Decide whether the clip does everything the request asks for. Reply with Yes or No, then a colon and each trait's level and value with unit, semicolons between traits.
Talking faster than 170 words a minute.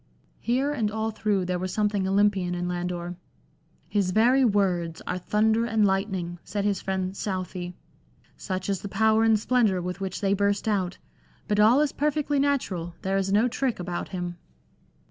Yes: average, 180 wpm